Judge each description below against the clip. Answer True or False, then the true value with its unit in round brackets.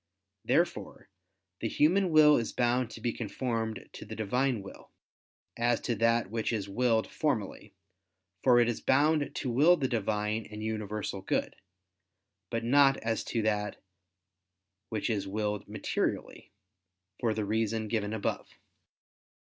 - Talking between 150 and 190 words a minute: False (140 wpm)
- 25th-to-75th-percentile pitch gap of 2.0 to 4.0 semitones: True (2.7 semitones)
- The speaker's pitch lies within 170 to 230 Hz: False (115 Hz)